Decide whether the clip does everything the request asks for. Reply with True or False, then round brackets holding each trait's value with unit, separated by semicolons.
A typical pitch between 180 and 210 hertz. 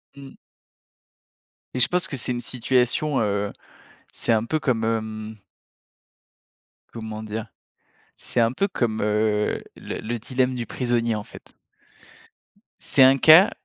False (115 Hz)